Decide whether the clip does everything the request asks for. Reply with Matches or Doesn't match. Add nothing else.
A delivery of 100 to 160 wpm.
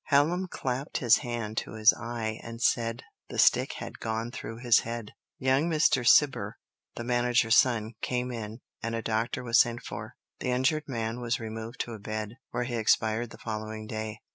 Doesn't match